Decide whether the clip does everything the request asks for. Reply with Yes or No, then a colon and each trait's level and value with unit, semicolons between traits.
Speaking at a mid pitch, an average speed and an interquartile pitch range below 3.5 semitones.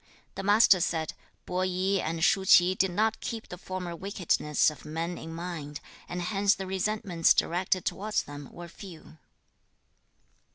Yes: medium, 180 Hz; average, 155 wpm; average, 2.7 semitones